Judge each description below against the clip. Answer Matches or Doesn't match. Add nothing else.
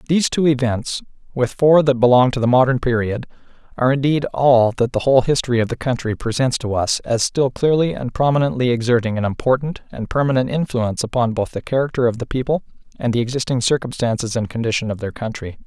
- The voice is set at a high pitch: Doesn't match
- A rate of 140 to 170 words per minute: Doesn't match